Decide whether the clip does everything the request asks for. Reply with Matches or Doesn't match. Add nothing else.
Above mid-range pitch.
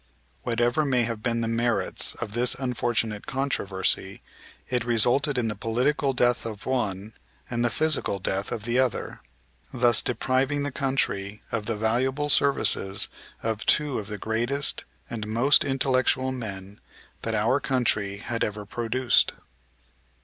Doesn't match